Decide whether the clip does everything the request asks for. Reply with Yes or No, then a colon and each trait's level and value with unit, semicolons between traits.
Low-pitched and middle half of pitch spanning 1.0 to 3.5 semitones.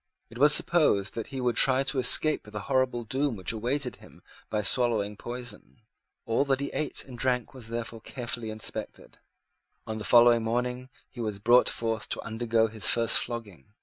Yes: low, 120 Hz; narrow, 2.5 semitones